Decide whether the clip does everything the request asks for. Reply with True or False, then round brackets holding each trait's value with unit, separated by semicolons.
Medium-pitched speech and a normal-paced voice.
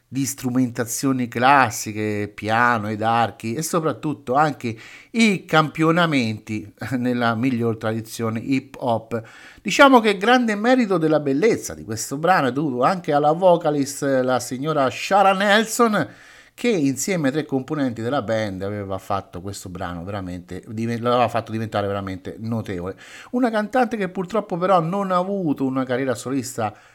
False (130 Hz; 140 wpm)